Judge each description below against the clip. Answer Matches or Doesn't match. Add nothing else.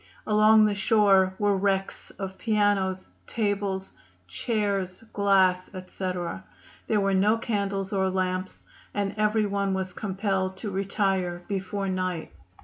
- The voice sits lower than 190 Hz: Doesn't match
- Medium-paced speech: Doesn't match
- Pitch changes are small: Matches